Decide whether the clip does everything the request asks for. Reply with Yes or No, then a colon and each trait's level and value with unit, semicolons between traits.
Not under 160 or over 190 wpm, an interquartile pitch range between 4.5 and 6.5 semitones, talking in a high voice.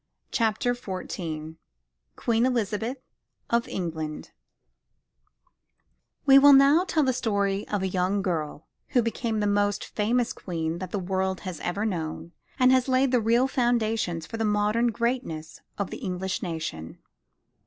No: average, 140 wpm; average, 5.0 semitones; high, 205 Hz